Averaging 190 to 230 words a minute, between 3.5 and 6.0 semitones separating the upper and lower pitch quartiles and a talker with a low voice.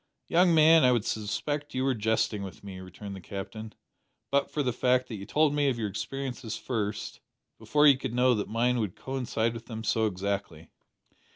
Yes: average, 195 wpm; average, 4.5 semitones; low, 115 Hz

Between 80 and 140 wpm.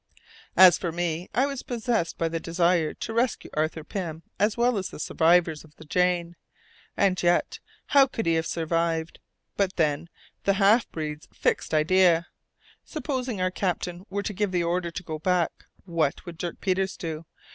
No: average, 175 wpm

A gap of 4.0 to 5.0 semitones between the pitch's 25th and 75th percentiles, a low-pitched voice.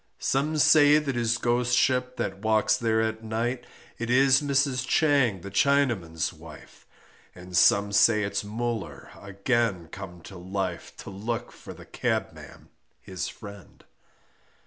Yes: average, 4.3 semitones; low, 115 Hz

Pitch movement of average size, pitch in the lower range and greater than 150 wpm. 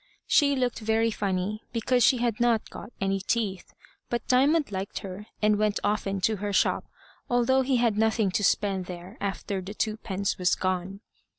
No: average, 3.4 semitones; high, 210 Hz; average, 175 wpm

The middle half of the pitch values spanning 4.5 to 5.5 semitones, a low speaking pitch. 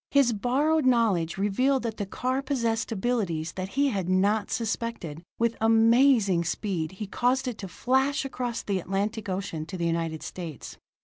No: average, 5.0 semitones; high, 220 Hz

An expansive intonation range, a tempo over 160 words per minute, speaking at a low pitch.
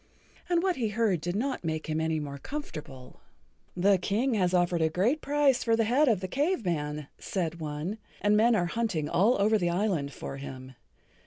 No: wide, 6.5 semitones; average, 195 wpm; medium, 185 Hz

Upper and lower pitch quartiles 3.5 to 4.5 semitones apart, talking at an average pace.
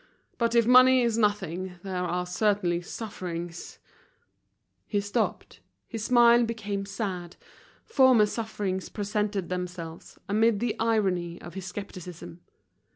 No: average, 3.9 semitones; slow, 115 wpm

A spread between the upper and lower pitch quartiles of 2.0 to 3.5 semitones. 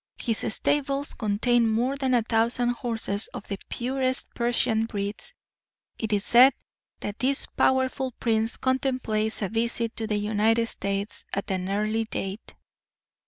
Yes: average, 3.0 semitones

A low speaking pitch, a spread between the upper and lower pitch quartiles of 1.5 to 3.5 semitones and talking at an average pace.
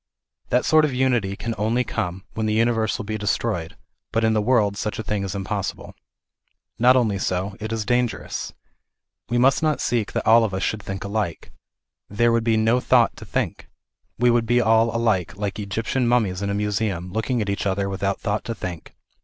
No: low, 110 Hz; average, 2.9 semitones; fast, 210 wpm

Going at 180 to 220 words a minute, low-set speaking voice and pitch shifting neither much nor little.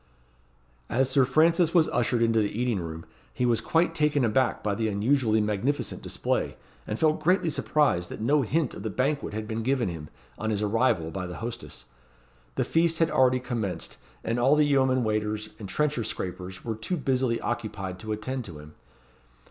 Yes: average, 185 wpm; low, 120 Hz; average, 4.7 semitones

